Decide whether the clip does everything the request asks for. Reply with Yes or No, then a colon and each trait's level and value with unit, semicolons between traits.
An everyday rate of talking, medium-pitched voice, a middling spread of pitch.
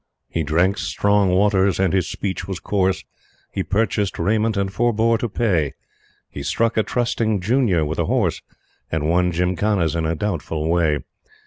No: average, 160 wpm; very low, 95 Hz; average, 3.8 semitones